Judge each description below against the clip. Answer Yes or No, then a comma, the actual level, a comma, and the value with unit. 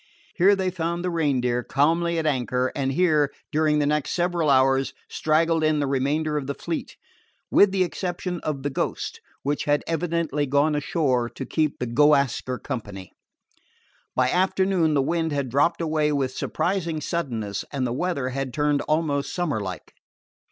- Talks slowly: No, average, 170 wpm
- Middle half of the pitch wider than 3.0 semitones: Yes, average, 3.7 semitones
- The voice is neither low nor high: Yes, medium, 150 Hz